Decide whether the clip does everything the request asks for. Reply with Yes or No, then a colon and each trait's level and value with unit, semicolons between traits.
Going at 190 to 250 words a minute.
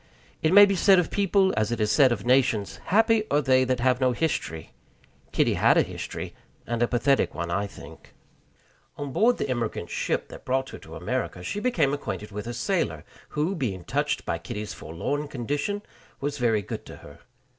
Yes: average, 195 wpm